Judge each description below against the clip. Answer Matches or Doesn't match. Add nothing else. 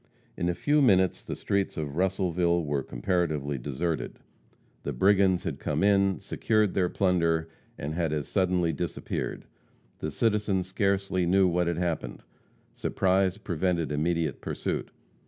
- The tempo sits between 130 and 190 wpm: Matches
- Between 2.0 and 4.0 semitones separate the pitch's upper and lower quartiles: Matches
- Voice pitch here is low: Matches